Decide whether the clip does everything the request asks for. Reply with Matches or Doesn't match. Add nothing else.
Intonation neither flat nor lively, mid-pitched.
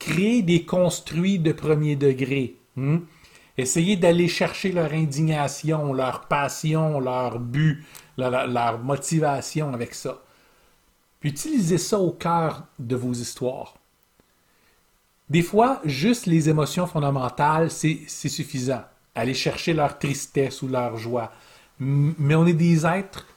Matches